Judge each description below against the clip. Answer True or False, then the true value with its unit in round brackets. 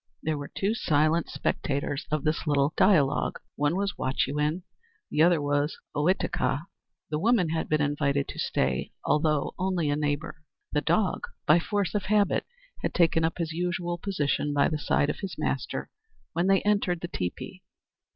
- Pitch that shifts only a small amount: False (3.5 semitones)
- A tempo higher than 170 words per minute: False (165 wpm)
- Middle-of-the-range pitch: True (160 Hz)